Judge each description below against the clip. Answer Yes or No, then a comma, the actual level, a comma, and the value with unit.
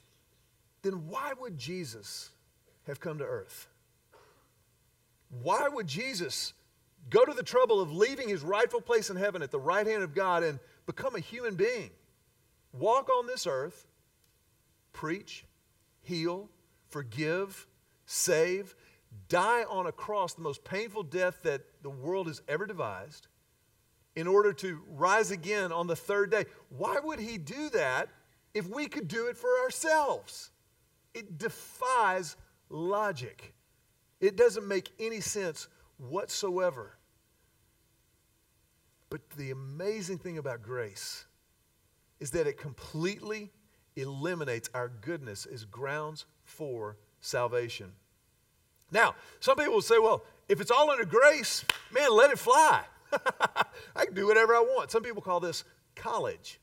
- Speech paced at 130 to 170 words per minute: Yes, slow, 135 wpm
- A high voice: Yes, high, 200 Hz